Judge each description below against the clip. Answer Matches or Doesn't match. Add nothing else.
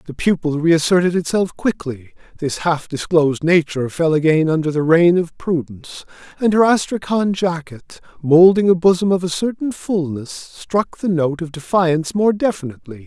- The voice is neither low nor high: Matches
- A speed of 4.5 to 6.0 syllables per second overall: Matches